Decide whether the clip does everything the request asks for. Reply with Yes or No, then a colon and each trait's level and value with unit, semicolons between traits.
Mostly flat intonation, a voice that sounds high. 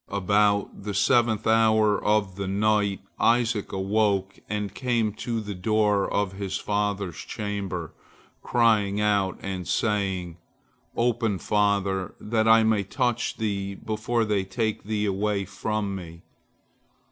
No: narrow, 1.9 semitones; low, 105 Hz